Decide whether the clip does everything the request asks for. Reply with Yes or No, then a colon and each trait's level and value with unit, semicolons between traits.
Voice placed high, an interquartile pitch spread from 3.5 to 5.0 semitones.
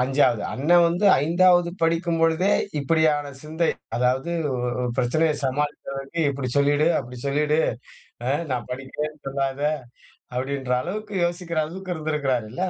No: medium, 150 Hz; average, 3.9 semitones